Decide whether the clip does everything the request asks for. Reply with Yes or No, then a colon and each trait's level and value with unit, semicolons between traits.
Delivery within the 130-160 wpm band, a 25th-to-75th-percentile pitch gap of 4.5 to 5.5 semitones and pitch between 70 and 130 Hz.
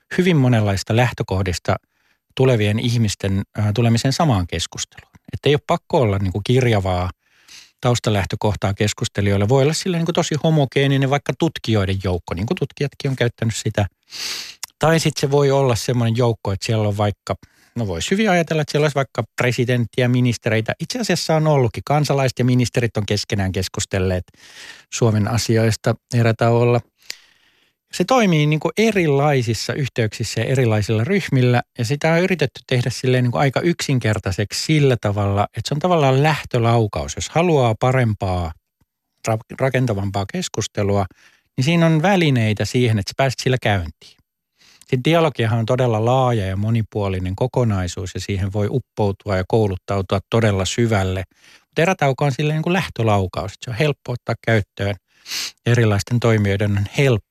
Yes: average, 150 wpm; average, 5.1 semitones; low, 120 Hz